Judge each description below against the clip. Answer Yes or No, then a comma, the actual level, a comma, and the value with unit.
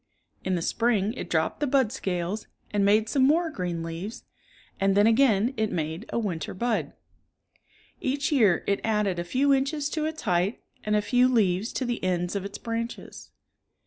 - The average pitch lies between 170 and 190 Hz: No, high, 215 Hz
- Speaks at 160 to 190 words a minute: Yes, average, 180 wpm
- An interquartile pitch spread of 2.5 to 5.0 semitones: No, wide, 5.4 semitones